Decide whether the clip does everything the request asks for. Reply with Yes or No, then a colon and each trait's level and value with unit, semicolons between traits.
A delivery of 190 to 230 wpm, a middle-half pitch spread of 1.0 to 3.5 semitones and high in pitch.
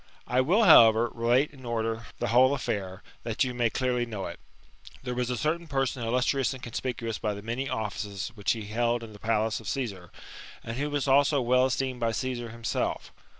No: average, 200 wpm; narrow, 2.6 semitones; low, 120 Hz